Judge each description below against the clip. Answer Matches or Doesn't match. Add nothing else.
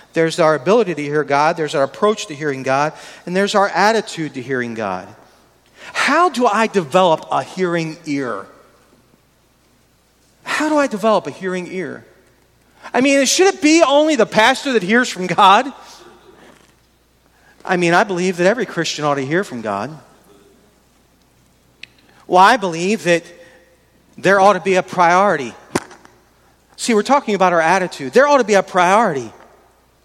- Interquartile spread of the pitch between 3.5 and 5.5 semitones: Matches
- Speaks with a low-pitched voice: Doesn't match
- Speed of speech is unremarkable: Matches